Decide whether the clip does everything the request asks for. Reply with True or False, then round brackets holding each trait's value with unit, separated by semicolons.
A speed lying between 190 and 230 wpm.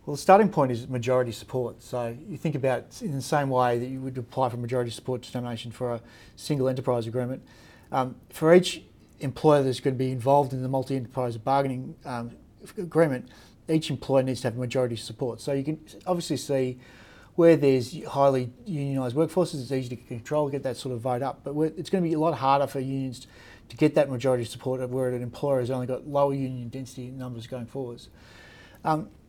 True (205 wpm)